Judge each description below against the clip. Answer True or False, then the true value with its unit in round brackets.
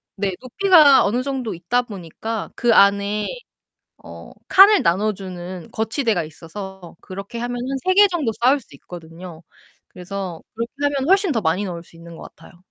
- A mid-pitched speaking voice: False (205 Hz)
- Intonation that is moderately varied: False (6.3 semitones)